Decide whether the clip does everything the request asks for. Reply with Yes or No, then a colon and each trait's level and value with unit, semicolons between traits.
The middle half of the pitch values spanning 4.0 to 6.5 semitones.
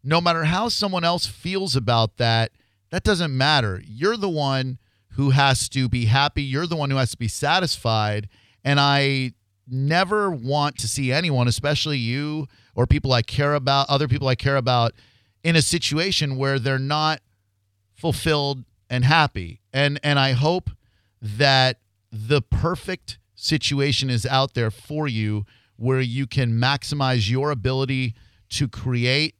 Yes: average, 4.4 semitones